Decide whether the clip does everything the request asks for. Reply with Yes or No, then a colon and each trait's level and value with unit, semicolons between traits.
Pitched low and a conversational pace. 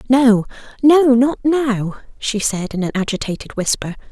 No: high, 235 Hz; average, 145 wpm